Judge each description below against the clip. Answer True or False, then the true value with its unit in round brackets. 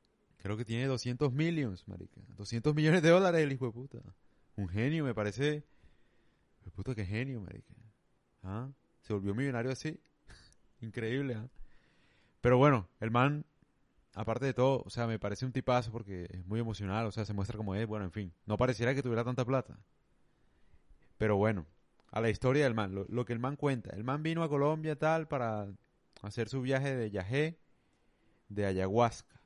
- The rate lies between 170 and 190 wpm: True (180 wpm)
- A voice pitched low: True (120 Hz)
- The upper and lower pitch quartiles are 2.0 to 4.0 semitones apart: False (4.4 semitones)